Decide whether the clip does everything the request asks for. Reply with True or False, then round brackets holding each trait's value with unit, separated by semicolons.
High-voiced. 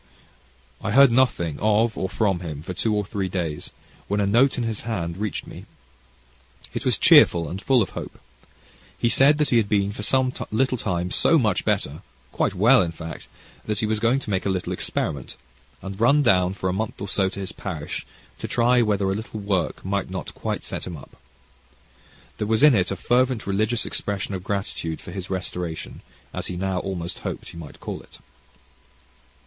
False (100 Hz)